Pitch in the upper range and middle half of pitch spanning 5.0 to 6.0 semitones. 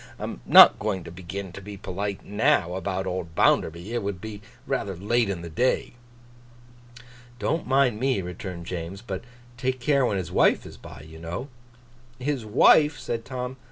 No: low, 100 Hz; wide, 5.6 semitones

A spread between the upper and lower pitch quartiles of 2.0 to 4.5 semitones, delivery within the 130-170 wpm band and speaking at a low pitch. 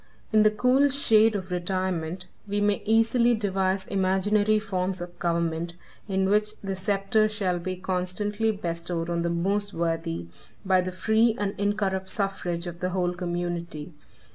No: average, 2.9 semitones; average, 150 wpm; high, 190 Hz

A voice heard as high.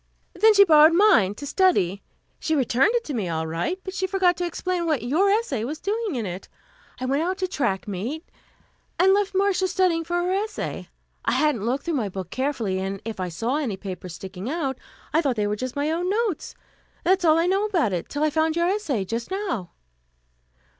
Yes: very high, 305 Hz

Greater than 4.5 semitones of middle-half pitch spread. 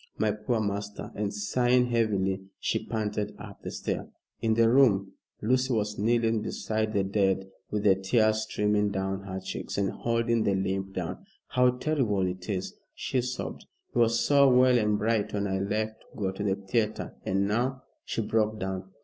No: average, 3.0 semitones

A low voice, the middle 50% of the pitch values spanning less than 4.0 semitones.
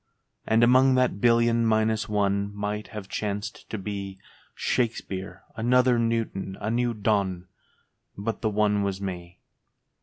Yes: low, 105 Hz; average, 2.7 semitones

